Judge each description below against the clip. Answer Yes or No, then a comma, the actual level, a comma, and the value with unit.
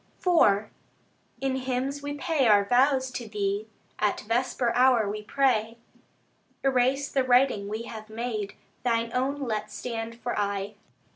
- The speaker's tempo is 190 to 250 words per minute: No, average, 140 wpm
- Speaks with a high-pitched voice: Yes, high, 240 Hz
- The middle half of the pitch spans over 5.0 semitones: No, average, 3.7 semitones